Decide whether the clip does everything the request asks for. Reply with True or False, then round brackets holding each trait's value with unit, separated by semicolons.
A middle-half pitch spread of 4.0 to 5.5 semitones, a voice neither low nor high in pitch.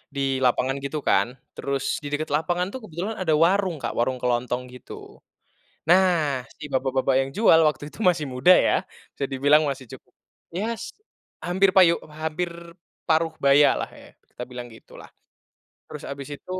True (4.7 semitones; 150 Hz)